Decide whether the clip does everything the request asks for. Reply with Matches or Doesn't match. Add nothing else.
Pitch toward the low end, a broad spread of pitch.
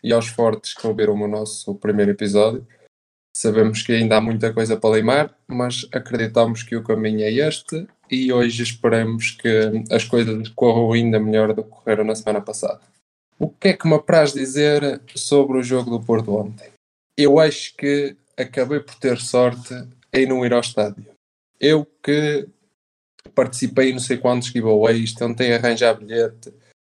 Doesn't match